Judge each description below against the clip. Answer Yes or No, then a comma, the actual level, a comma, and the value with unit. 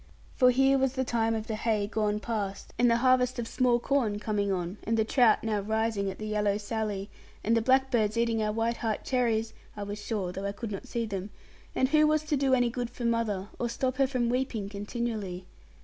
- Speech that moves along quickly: Yes, fast, 225 wpm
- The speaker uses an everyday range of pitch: Yes, average, 3.0 semitones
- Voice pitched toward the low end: No, high, 225 Hz